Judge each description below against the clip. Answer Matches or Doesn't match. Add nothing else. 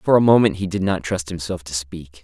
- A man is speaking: Matches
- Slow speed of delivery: Doesn't match